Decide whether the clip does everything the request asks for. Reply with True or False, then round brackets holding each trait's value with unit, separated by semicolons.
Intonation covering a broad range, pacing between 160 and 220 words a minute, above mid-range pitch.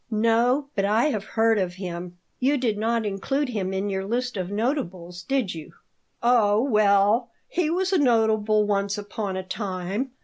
False (4.0 semitones; 170 wpm; 215 Hz)